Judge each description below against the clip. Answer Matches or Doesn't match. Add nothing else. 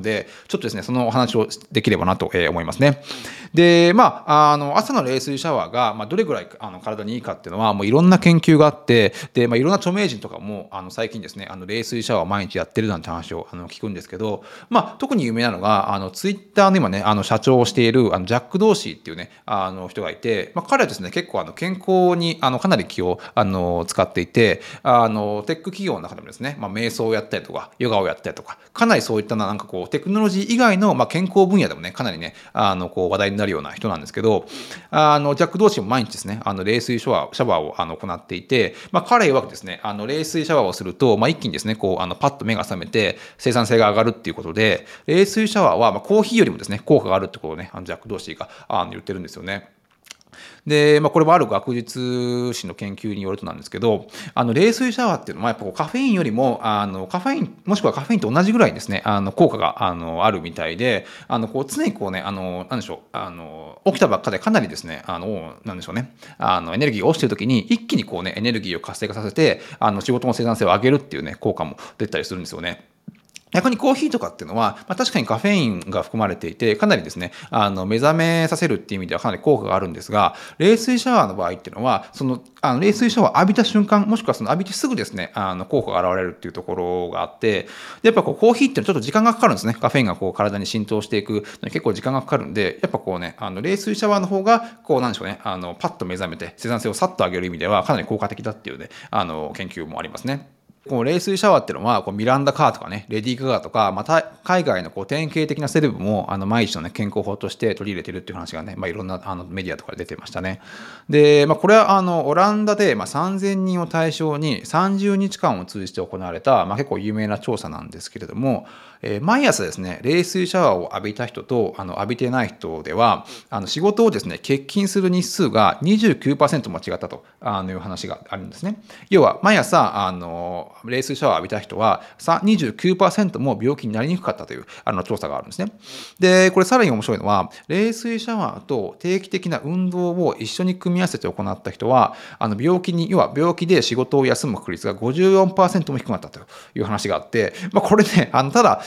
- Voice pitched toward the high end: Doesn't match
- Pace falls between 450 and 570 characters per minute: Matches